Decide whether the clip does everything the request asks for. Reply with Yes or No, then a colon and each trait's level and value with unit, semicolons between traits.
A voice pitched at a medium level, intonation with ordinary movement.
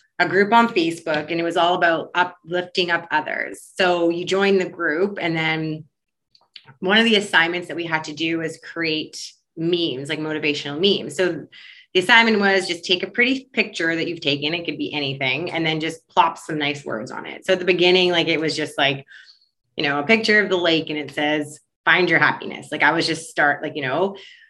Yes: medium, 170 Hz; average, 3.3 semitones